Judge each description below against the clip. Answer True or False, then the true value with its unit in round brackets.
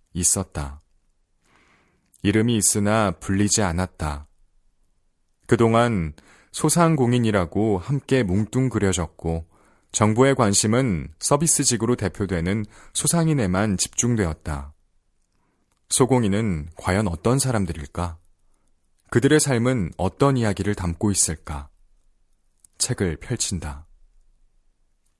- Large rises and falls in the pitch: True (5.8 semitones)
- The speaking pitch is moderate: False (100 Hz)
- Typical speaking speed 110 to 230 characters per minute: True (220 characters per minute)